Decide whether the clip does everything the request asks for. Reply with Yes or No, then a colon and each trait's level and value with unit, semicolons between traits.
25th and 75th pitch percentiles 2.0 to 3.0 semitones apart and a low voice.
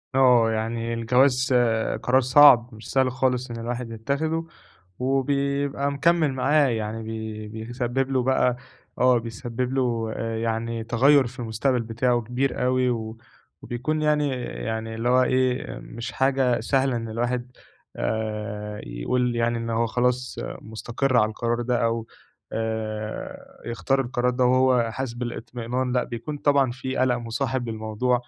Yes: narrow, 2.4 semitones; low, 120 Hz